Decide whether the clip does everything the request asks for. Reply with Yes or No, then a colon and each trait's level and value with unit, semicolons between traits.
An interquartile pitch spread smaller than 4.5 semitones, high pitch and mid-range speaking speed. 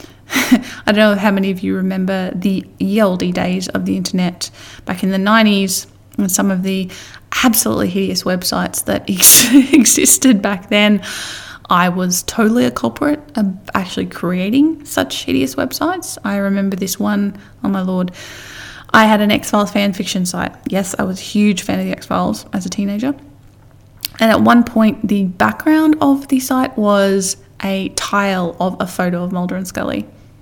Yes: average, 3.4 semitones; high, 200 Hz; average, 170 wpm